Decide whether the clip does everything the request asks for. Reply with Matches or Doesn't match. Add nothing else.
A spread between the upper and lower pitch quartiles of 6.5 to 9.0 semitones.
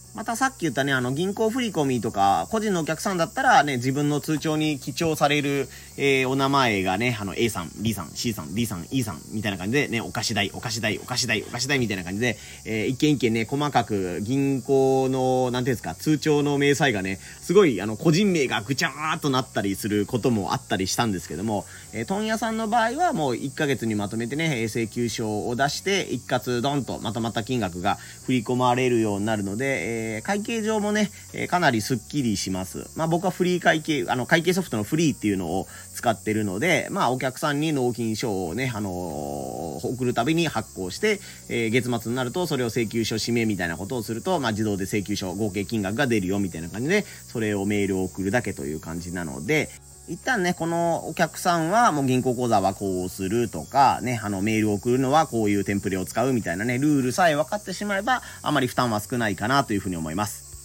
Doesn't match